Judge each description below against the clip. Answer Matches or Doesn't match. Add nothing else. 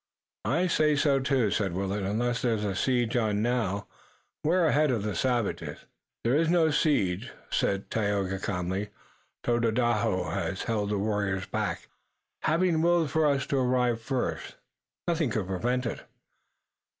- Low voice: Matches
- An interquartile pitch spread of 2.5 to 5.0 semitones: Doesn't match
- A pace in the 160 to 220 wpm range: Doesn't match